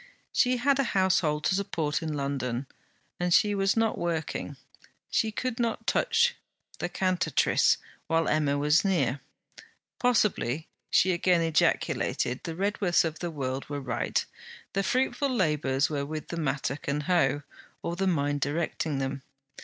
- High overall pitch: No, medium, 165 Hz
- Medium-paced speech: Yes, average, 145 wpm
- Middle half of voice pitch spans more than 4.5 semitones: Yes, average, 5.3 semitones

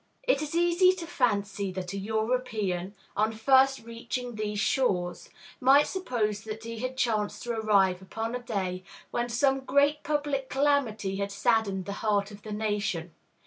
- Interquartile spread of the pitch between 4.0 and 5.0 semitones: Yes, average, 4.7 semitones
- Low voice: No, high, 220 Hz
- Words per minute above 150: Yes, average, 160 wpm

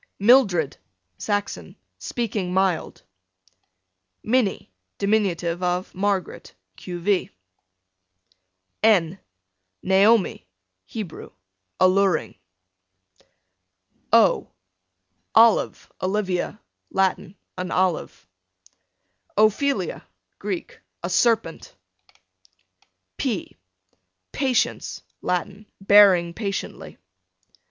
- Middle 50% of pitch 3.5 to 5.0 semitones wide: No, average, 2.9 semitones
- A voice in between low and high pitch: No, high, 195 Hz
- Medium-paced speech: No, slow, 65 wpm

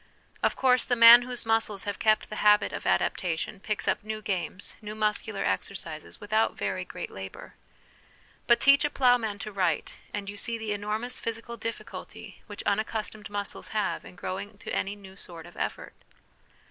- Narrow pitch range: Yes, narrow, 2.3 semitones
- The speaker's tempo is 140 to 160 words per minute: No, average, 170 wpm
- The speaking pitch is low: No, high, 210 Hz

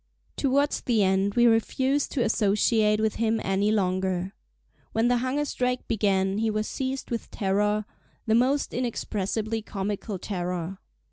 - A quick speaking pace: No, slow, 135 wpm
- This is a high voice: Yes, high, 215 Hz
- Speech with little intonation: No, average, 3.6 semitones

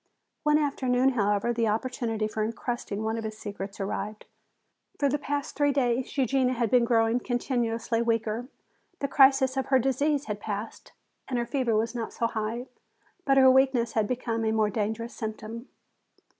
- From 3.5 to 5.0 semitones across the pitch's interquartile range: No, average, 3.0 semitones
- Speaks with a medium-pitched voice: No, high, 235 Hz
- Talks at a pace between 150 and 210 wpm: Yes, average, 170 wpm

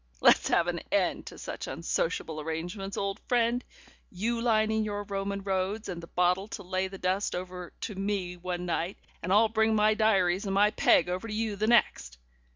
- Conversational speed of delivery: Yes, average, 190 wpm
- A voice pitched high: Yes, high, 195 Hz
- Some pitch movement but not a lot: Yes, average, 3.1 semitones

